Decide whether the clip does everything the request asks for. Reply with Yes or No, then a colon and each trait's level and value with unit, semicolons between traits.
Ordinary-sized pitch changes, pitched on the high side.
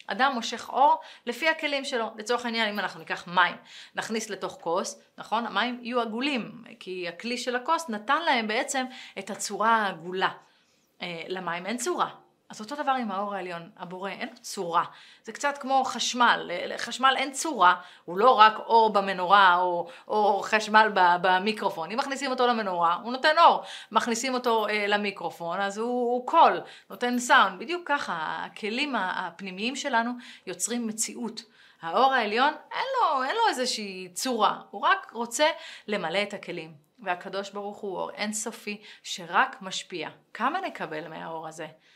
Yes: average, 4.9 semitones; high, 225 Hz